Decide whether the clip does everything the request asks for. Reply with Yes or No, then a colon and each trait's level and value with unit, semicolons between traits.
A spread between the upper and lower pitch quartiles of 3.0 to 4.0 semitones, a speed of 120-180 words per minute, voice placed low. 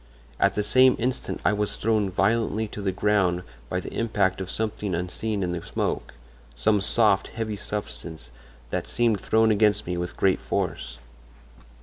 Yes: average, 3.3 semitones; average, 155 wpm; low, 105 Hz